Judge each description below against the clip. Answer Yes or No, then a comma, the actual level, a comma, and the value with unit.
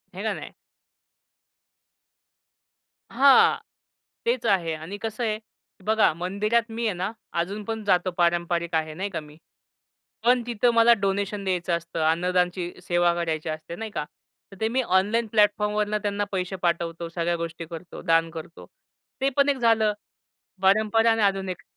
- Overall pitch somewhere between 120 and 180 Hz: No, high, 190 Hz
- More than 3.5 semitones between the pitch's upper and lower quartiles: Yes, average, 4.2 semitones